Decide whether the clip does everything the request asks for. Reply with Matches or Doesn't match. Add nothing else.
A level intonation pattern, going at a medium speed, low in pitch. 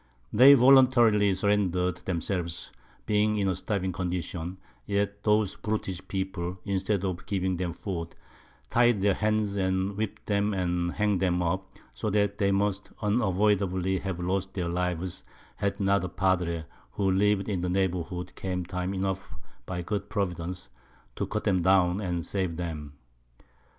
Matches